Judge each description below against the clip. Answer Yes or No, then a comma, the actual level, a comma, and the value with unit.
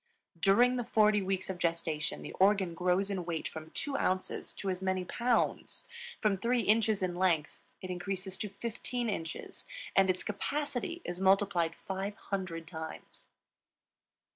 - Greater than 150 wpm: No, average, 145 wpm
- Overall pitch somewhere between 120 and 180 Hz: No, high, 190 Hz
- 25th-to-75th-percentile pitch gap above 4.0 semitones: No, average, 2.9 semitones